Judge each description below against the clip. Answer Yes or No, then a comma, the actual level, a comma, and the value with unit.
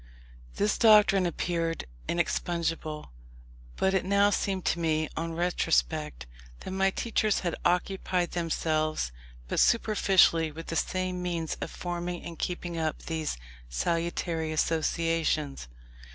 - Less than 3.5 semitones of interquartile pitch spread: Yes, narrow, 2.5 semitones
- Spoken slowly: Yes, slow, 115 wpm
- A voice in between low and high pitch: Yes, medium, 170 Hz